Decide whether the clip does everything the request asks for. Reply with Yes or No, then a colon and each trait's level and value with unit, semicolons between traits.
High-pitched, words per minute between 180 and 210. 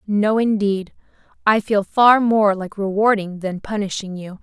No: high, 205 Hz; average, 150 wpm